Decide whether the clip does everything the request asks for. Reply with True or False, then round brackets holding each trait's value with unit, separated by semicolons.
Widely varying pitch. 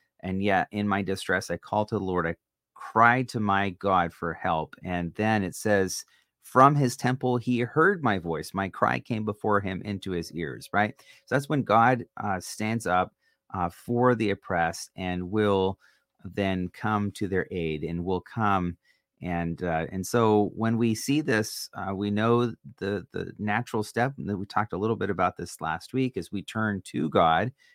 False (3.8 semitones)